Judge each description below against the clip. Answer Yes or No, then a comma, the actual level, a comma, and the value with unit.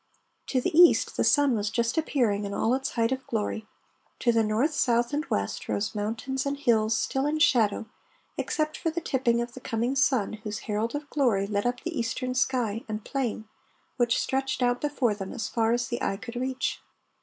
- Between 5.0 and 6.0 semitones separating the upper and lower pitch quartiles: No, average, 3.5 semitones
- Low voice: No, high, 240 Hz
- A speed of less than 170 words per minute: No, average, 200 wpm